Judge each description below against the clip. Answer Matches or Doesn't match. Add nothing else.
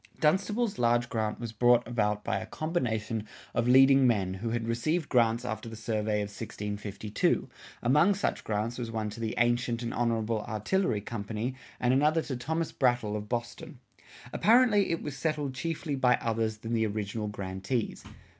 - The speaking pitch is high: Doesn't match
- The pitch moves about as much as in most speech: Matches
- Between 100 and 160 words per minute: Doesn't match